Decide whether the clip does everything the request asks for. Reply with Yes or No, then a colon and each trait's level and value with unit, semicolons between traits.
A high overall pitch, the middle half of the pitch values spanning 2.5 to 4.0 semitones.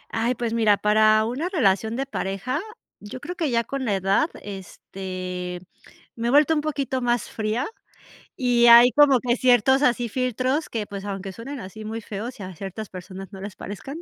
No: high, 230 Hz; average, 4.5 semitones